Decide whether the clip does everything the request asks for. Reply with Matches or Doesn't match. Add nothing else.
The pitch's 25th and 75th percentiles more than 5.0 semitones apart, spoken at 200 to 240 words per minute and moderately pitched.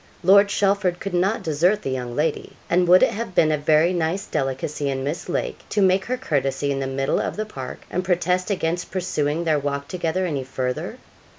Doesn't match